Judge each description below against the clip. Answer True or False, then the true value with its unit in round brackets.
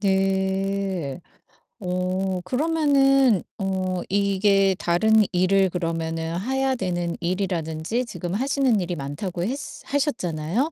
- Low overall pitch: False (190 Hz)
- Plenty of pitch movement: False (3.8 semitones)